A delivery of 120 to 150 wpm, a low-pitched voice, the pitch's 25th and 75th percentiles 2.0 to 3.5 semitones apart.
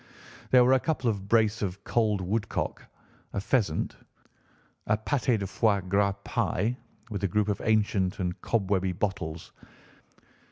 Yes: average, 145 wpm; low, 105 Hz; average, 2.7 semitones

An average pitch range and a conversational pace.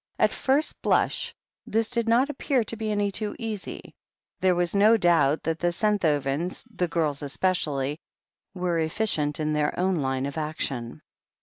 No: wide, 6.1 semitones; average, 165 wpm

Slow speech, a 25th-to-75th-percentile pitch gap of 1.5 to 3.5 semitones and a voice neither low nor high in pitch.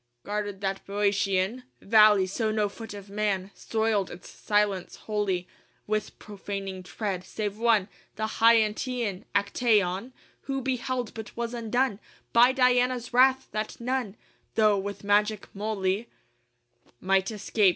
No: slow, 130 wpm; average, 2.8 semitones; high, 210 Hz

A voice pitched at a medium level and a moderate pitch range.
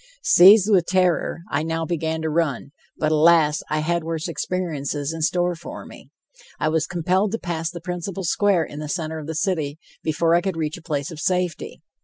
No: medium, 165 Hz; narrow, 2.3 semitones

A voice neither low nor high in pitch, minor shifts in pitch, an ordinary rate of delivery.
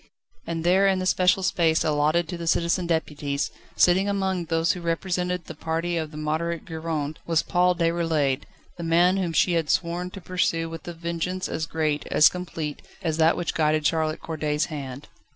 Yes: medium, 165 Hz; narrow, 2.2 semitones; average, 185 wpm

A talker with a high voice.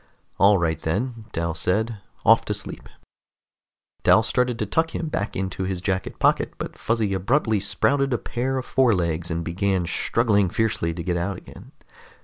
No: low, 100 Hz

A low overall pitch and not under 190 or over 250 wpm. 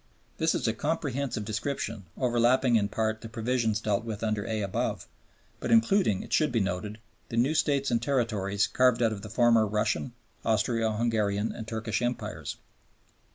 No: low, 115 Hz; average, 165 wpm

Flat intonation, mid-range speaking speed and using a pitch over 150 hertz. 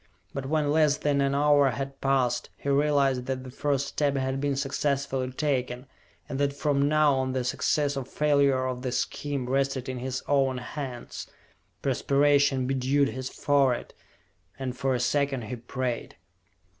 No: narrow, 1.7 semitones; average, 160 wpm; low, 135 Hz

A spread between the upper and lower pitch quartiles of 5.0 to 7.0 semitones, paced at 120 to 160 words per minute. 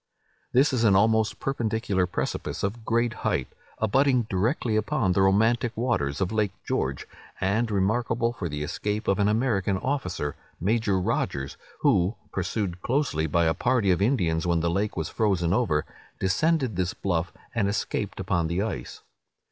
No: average, 4.6 semitones; average, 155 wpm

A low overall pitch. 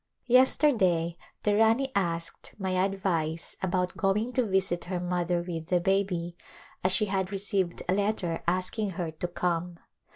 No: medium, 185 Hz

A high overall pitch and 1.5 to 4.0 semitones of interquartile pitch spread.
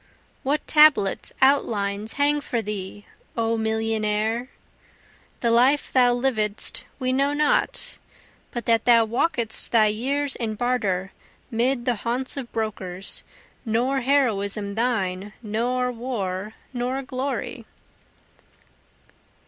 Yes: high, 235 Hz; average, 3.4 semitones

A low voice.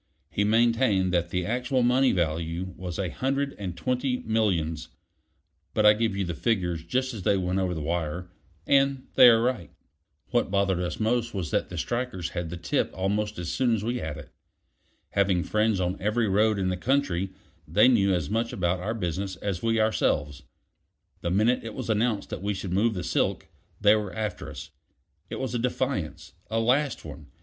Yes: low, 100 Hz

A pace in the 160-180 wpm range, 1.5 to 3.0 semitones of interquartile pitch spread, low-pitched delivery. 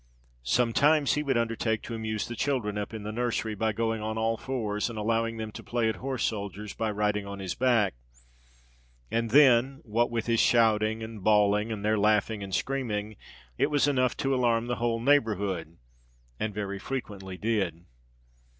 Yes: average, 175 wpm; narrow, 2.4 semitones; low, 110 Hz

